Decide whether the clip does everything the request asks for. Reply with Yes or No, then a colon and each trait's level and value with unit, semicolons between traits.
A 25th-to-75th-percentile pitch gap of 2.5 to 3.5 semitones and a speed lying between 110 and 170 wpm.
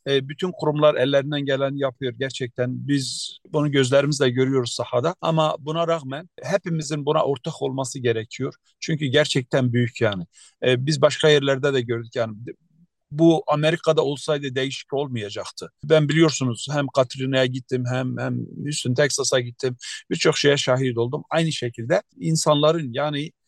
Yes: average, 3.2 semitones; average, 135 wpm